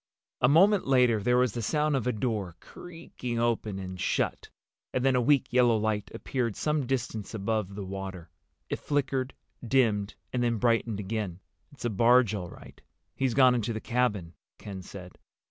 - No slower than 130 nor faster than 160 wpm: No, average, 175 wpm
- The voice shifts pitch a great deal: No, average, 3.8 semitones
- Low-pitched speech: Yes, low, 115 Hz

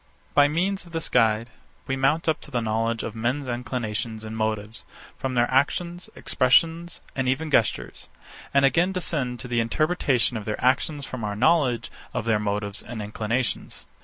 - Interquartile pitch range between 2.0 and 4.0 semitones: No, average, 4.7 semitones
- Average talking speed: Yes, average, 170 wpm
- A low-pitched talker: Yes, low, 125 Hz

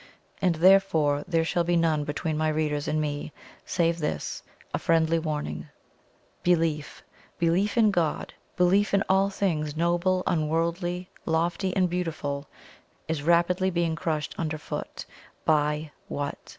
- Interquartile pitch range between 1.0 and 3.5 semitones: Yes, narrow, 2.6 semitones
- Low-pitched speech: No, medium, 165 Hz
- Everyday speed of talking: No, slow, 130 wpm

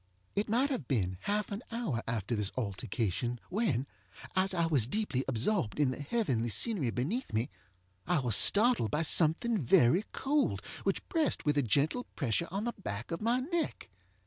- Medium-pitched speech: Yes, medium, 155 Hz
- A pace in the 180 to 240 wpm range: No, average, 170 wpm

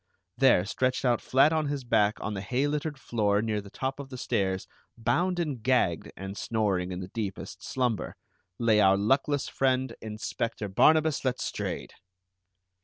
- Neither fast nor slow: Yes, average, 160 wpm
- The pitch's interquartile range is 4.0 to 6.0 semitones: Yes, average, 4.8 semitones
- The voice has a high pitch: No, low, 120 Hz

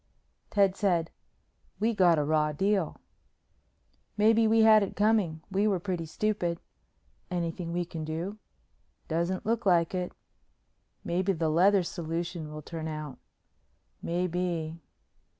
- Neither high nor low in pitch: Yes, medium, 175 Hz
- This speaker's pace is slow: Yes, slow, 125 wpm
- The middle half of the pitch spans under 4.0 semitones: Yes, average, 3.5 semitones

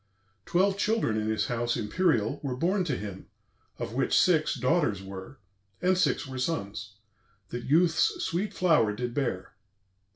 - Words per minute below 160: Yes, average, 150 wpm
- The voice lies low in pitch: Yes, low, 130 Hz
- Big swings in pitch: Yes, wide, 8.0 semitones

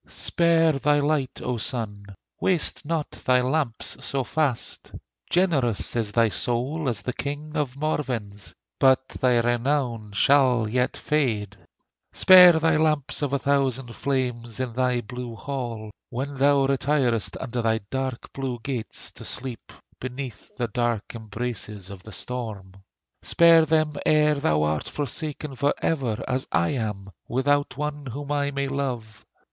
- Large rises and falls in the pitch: No, average, 3.7 semitones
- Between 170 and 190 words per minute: No, average, 145 wpm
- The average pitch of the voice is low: Yes, low, 130 Hz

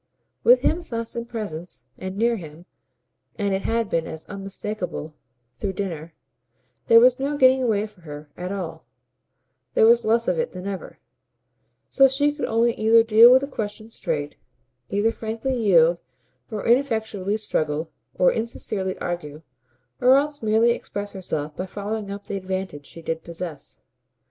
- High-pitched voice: Yes, high, 205 Hz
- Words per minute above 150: Yes, average, 160 wpm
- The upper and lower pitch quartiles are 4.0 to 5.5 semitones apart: Yes, average, 4.6 semitones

